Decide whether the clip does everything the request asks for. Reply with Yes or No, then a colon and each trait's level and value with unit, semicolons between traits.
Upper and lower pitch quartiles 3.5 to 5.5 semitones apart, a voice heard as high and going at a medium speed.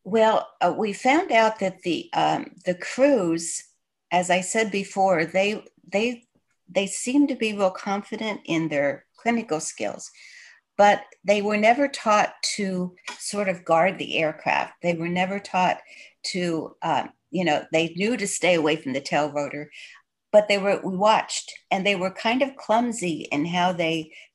Yes: average, 4.4 semitones; high, 195 Hz; average, 170 wpm